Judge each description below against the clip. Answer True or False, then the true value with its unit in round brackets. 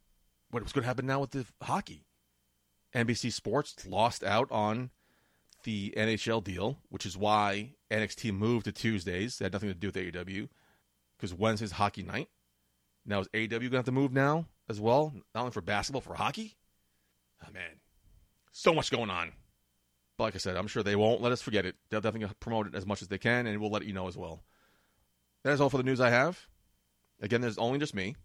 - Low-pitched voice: True (105 Hz)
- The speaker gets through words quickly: True (210 wpm)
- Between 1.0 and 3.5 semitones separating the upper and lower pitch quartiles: False (3.9 semitones)